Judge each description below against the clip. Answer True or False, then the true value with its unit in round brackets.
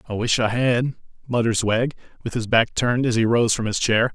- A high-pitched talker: False (115 Hz)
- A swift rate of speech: True (230 wpm)